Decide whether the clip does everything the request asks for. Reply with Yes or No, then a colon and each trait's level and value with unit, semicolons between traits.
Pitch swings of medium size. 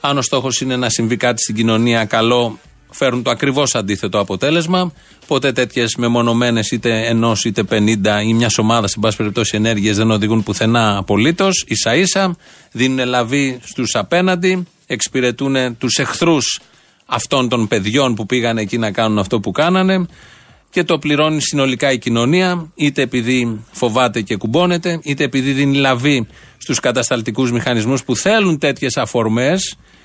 Yes: average, 3.8 semitones